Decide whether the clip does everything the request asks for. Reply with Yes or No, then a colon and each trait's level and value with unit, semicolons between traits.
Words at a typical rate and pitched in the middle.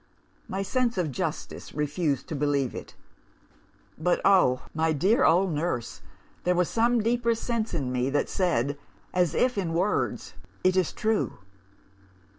Yes: average, 145 wpm; medium, 180 Hz